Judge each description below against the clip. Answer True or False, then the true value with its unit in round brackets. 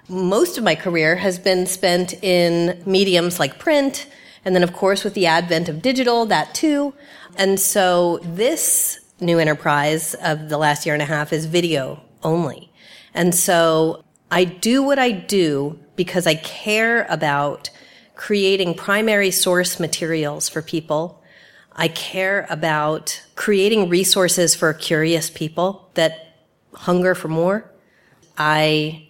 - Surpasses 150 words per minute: False (140 wpm)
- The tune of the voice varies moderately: True (3.4 semitones)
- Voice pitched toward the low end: False (175 Hz)